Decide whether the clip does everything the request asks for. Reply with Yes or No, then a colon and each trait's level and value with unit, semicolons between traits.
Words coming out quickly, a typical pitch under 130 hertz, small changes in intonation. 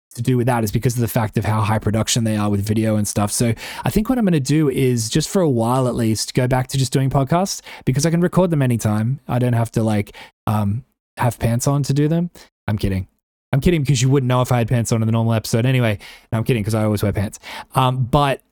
No: fast, 280 wpm; low, 120 Hz; average, 3.9 semitones